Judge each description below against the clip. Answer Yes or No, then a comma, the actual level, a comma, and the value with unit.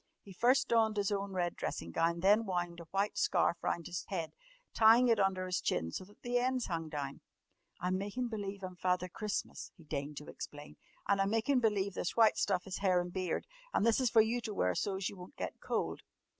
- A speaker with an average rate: No, fast, 225 wpm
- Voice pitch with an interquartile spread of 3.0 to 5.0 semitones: Yes, average, 3.7 semitones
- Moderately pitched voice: No, high, 195 Hz